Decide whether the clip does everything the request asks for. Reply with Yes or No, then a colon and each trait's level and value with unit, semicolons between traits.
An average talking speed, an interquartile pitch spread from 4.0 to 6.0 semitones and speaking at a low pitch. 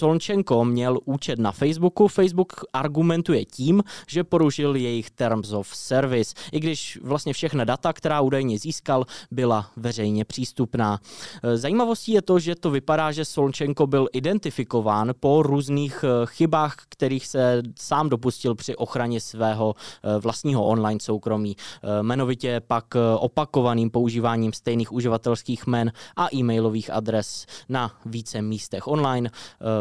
Yes: average, 125 wpm; average, 4.6 semitones; low, 125 Hz